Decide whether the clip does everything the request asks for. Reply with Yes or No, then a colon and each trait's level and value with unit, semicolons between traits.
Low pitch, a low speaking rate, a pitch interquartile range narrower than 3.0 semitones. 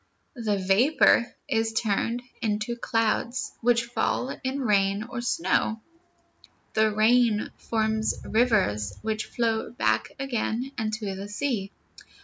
No: high, 225 Hz; slow, 115 wpm; narrow, 2.4 semitones